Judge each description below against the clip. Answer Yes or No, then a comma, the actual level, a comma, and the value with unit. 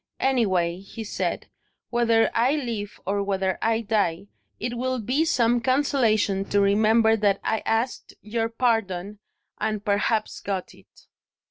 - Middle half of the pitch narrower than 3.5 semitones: Yes, average, 2.9 semitones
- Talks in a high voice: Yes, high, 220 Hz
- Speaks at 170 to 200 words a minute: No, slow, 135 wpm